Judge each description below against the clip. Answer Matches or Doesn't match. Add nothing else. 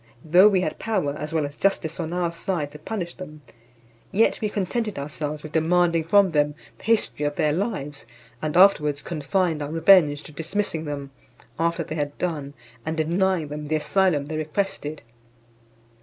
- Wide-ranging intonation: Doesn't match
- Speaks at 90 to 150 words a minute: Doesn't match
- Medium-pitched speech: Matches